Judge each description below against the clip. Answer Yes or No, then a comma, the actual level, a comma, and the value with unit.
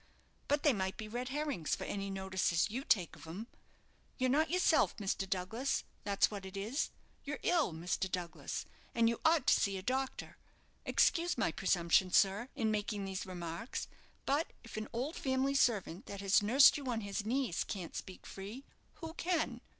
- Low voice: No, high, 215 Hz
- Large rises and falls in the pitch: Yes, wide, 6.0 semitones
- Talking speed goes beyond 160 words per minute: Yes, average, 180 wpm